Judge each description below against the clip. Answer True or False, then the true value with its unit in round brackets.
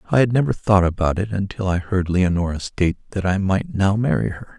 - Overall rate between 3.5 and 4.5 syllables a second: False (5.7 syllables/s)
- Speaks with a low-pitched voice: True (100 Hz)